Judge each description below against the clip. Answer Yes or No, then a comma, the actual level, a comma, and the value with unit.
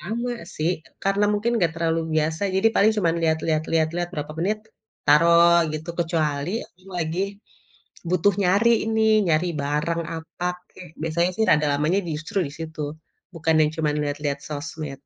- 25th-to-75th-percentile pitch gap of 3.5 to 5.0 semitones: No, average, 2.8 semitones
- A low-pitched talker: No, medium, 165 Hz